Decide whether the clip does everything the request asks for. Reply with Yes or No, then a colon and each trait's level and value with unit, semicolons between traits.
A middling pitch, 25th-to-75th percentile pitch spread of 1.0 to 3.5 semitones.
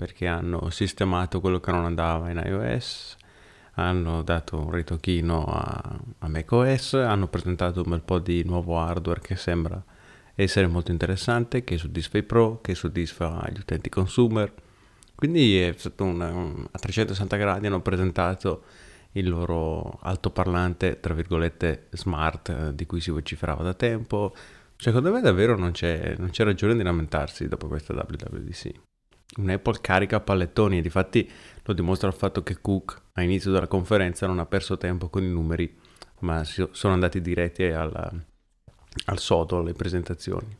No: very low, 90 Hz; average, 2.8 semitones